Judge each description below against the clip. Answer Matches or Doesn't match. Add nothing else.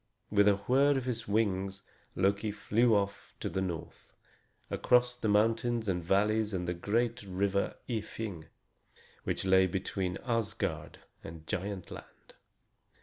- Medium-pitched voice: Doesn't match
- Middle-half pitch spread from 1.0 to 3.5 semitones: Matches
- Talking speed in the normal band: Doesn't match